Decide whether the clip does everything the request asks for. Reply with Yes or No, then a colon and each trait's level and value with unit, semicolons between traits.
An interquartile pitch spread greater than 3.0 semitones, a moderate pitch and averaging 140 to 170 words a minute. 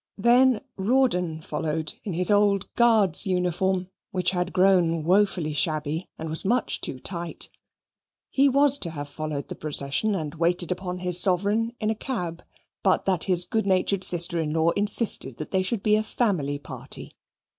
Yes: average, 4.2 semitones; medium, 180 Hz; average, 165 wpm